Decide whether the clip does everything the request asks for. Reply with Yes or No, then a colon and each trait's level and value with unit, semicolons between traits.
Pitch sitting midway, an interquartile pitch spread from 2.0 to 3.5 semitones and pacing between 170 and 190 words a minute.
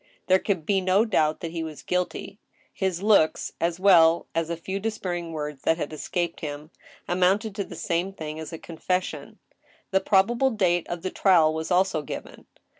Yes: medium, 175 Hz; average, 2.9 semitones; average, 185 wpm